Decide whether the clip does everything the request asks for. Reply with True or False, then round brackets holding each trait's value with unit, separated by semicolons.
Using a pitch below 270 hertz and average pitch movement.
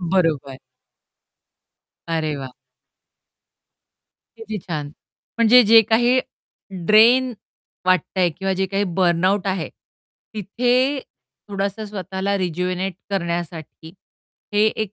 True (190 Hz; 3.9 semitones)